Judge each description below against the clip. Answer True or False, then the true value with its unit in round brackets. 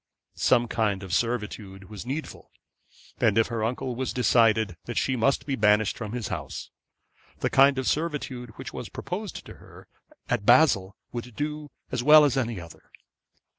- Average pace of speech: True (165 wpm)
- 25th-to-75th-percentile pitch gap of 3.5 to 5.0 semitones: True (3.8 semitones)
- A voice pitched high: False (120 Hz)